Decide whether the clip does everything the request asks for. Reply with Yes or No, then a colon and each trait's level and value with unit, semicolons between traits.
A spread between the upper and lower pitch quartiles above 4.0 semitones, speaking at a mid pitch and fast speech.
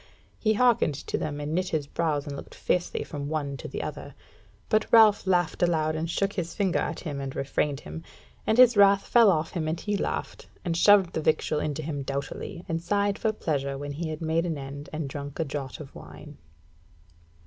Yes: average, 4.7 semitones; medium, 160 Hz; fast, 210 wpm